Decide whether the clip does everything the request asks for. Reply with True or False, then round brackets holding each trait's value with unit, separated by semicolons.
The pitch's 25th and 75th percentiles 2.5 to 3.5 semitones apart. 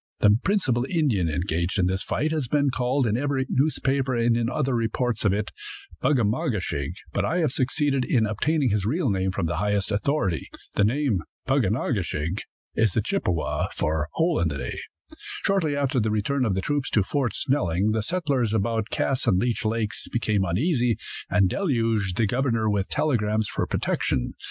False (5.4 semitones)